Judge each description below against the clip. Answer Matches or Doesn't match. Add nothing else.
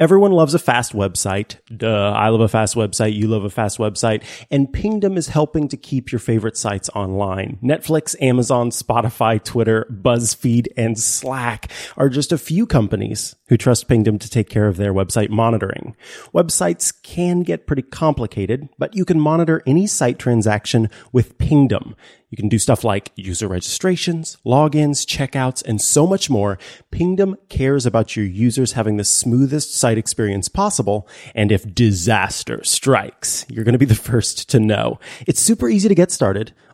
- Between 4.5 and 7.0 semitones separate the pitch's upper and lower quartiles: Matches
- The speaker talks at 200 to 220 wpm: Doesn't match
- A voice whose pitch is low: Matches